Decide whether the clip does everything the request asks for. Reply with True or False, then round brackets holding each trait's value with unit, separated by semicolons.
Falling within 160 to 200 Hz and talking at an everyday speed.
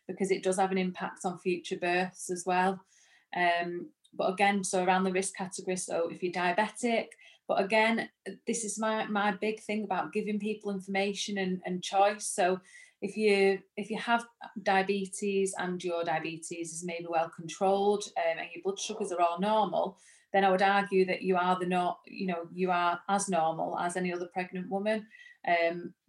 True (190 Hz; 185 wpm)